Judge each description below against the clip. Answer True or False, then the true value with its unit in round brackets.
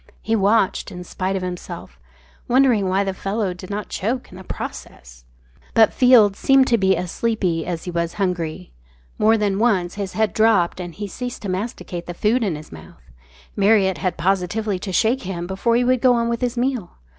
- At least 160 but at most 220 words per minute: True (200 wpm)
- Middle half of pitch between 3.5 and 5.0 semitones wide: True (4.0 semitones)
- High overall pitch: True (195 Hz)